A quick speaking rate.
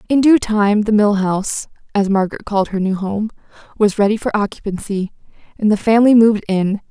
No: average, 185 wpm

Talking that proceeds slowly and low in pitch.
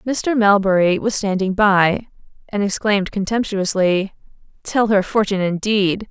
No: slow, 120 wpm; high, 200 Hz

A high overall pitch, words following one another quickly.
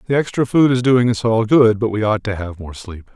No: low, 110 Hz; fast, 285 wpm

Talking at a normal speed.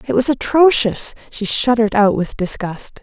Yes: average, 160 wpm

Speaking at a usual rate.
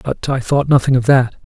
No: fast, 230 wpm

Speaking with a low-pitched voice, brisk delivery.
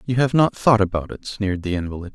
Yes: low, 105 Hz; fast, 250 wpm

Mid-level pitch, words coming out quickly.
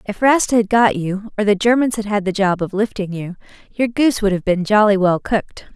No: high, 205 Hz; fast, 240 wpm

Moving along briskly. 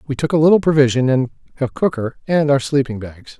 Yes: fast, 210 wpm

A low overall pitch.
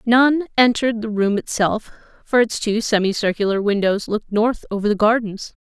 No: high, 220 Hz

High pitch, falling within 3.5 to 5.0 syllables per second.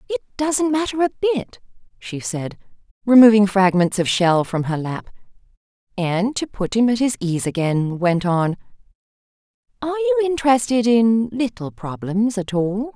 Yes: high, 220 Hz; 4.6 syllables/s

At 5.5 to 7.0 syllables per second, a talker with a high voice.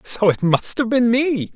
No: 4.1 syllables/s; high, 225 Hz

